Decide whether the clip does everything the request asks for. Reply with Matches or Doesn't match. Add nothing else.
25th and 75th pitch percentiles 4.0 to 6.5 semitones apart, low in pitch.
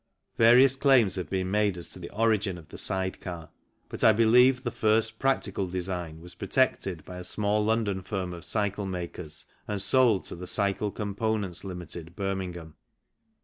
Doesn't match